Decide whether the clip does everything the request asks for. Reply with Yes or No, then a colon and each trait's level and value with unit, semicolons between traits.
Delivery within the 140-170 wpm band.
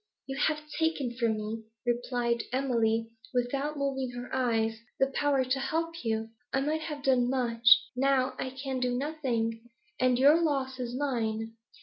Yes: average, 155 wpm